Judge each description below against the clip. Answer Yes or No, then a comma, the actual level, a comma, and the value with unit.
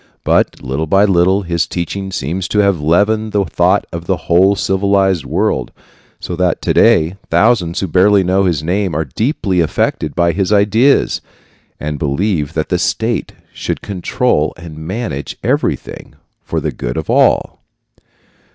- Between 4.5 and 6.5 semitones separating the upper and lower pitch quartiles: No, average, 3.7 semitones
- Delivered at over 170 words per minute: No, average, 155 wpm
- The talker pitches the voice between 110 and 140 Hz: No, very low, 90 Hz